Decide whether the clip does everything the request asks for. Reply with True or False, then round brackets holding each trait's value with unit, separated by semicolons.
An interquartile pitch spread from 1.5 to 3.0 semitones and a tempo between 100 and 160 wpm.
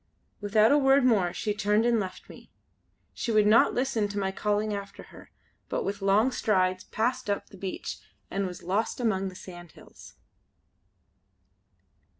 True (2.7 semitones; 155 wpm)